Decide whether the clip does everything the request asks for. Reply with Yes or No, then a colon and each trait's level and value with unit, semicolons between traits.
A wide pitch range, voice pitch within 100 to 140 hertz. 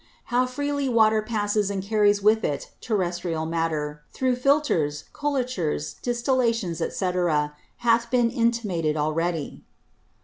No: wide, 6.7 semitones; high, 215 Hz